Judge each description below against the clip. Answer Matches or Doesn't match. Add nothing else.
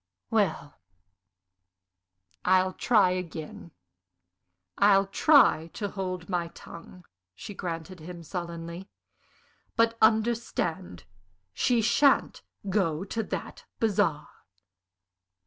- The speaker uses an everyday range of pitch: Matches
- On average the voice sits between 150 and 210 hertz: Matches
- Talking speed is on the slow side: Matches